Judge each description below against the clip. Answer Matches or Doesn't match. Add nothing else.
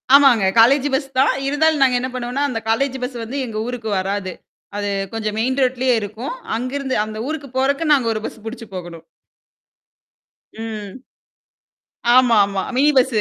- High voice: Matches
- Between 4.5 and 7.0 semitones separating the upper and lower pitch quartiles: Doesn't match